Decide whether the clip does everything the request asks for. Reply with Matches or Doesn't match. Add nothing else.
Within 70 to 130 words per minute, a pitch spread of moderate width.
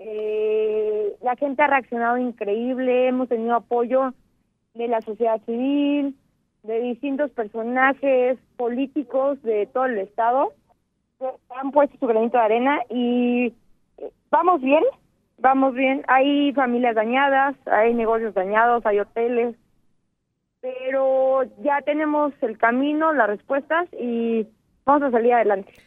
Matches